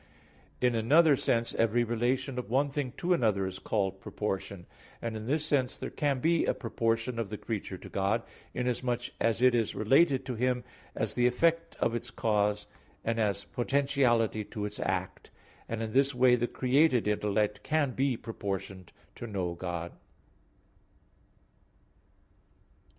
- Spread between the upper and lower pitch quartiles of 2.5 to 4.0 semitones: Yes, average, 3.7 semitones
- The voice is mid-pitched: No, low, 120 Hz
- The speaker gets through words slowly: No, average, 155 wpm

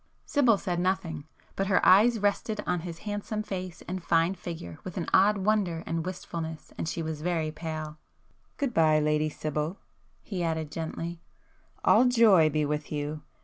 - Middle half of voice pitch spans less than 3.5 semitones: No, average, 3.9 semitones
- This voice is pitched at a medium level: Yes, medium, 170 Hz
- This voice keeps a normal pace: Yes, average, 155 wpm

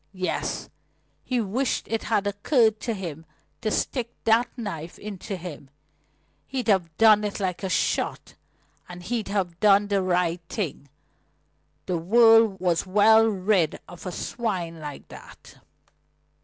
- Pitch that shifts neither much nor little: Yes, average, 3.8 semitones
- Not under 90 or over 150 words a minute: Yes, average, 140 wpm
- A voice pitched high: Yes, high, 200 Hz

